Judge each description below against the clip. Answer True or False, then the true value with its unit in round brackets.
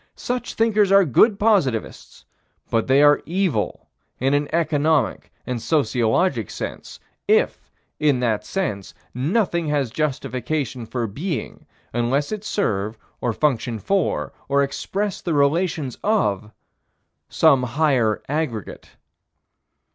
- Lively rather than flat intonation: True (6.3 semitones)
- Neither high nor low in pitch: True (145 Hz)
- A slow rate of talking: True (115 wpm)